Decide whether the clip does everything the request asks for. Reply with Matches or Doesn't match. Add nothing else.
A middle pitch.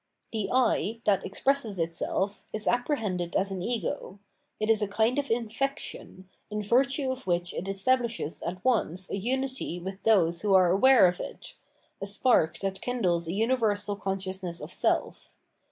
Doesn't match